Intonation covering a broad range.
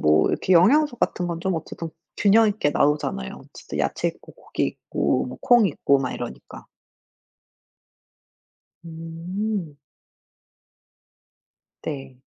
Yes: wide, 6.2 semitones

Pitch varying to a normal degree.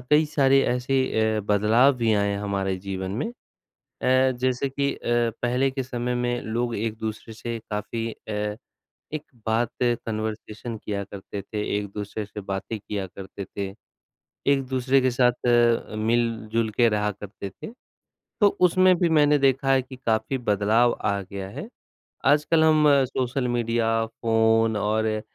Yes: average, 3.5 semitones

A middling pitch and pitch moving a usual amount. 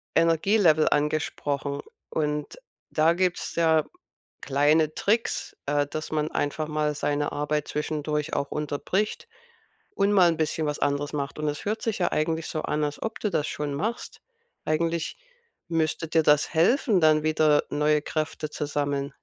No: medium, 155 Hz; narrow, 1.9 semitones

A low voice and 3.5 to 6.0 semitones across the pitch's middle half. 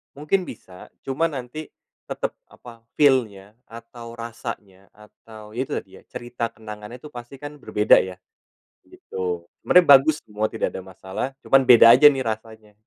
Yes: low, 115 Hz; average, 4.0 semitones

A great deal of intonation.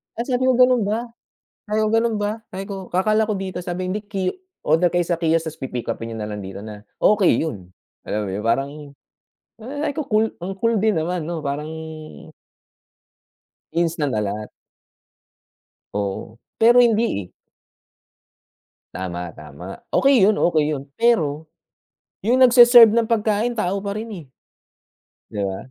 Yes: wide, 7.8 semitones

